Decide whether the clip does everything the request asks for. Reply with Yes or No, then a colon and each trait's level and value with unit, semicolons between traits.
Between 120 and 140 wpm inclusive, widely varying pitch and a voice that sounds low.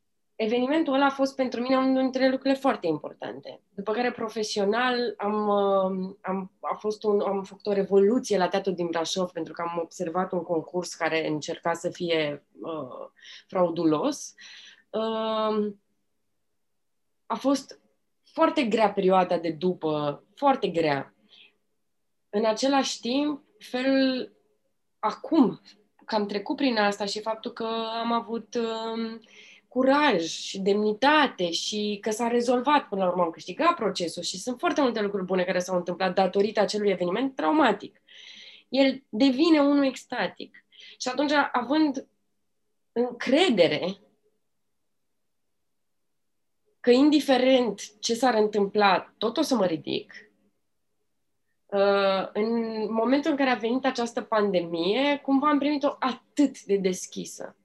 No: average, 130 wpm; wide, 5.8 semitones; high, 215 Hz